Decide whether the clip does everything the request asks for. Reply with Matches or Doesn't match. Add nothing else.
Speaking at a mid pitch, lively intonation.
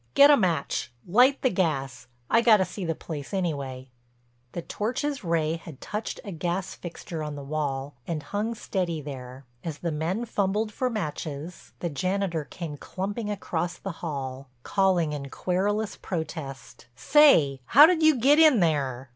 Matches